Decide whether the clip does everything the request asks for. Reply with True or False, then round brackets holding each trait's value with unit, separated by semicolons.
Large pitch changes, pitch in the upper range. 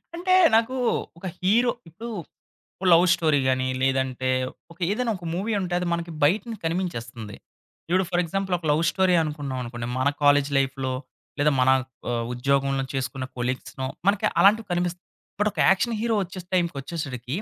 False (6.1 semitones; 165 Hz)